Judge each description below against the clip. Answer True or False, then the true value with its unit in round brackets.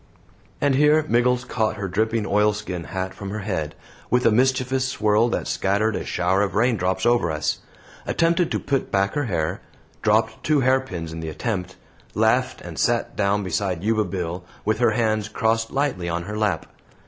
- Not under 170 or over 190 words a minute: True (175 wpm)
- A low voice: True (105 Hz)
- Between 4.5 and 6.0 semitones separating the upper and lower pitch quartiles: True (4.8 semitones)